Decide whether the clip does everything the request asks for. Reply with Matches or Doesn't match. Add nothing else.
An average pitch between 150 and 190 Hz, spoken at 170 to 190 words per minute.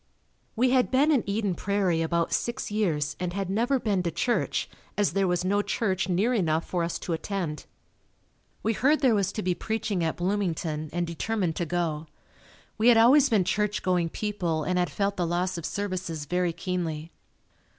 Matches